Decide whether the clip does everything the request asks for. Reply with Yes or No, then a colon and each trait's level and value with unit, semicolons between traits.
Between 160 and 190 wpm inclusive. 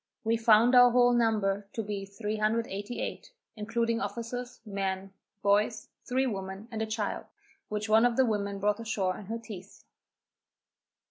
No: average, 145 wpm